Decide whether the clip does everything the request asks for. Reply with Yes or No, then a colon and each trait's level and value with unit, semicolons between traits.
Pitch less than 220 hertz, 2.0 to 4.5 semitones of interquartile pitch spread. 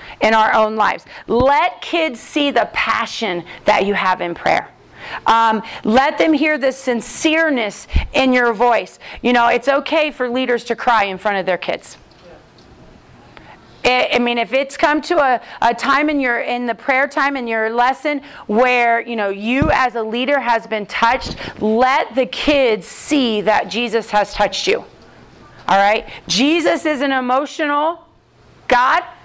No: high, 245 Hz; average, 4.1 semitones